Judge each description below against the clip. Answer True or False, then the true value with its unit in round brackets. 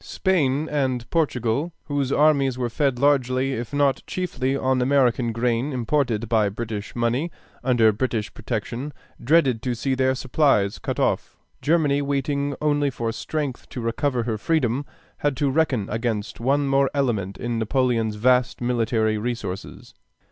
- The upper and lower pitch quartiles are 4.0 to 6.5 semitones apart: False (3.5 semitones)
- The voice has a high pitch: False (130 Hz)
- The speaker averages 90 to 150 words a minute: True (145 wpm)